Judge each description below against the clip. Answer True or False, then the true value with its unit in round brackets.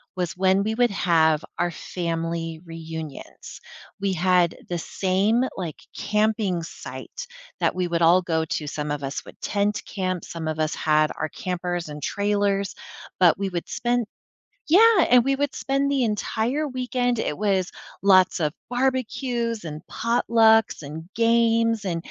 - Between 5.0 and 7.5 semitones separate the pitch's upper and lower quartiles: True (5.6 semitones)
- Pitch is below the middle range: False (190 Hz)